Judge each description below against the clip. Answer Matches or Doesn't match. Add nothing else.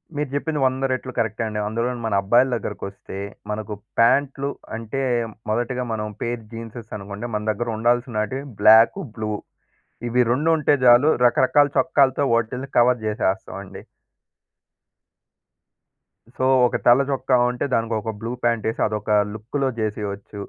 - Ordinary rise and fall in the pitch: Matches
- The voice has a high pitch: Doesn't match